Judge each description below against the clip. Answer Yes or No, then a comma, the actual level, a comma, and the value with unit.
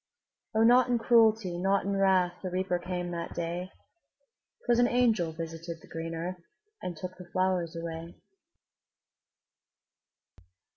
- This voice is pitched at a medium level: Yes, medium, 180 Hz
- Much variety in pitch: No, average, 2.8 semitones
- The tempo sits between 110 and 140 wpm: Yes, slow, 135 wpm